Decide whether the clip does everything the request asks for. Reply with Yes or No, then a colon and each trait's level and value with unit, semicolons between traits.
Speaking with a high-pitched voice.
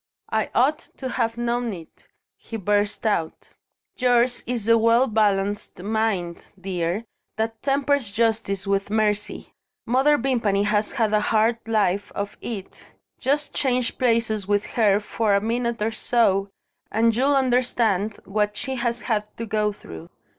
Yes: high, 220 Hz